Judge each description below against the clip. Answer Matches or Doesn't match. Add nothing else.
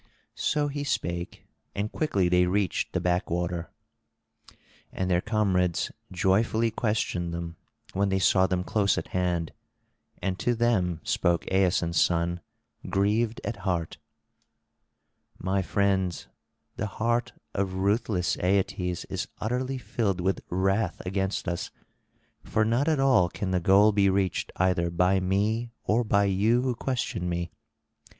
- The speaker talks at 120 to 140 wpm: Matches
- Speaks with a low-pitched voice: Matches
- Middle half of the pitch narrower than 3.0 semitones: Doesn't match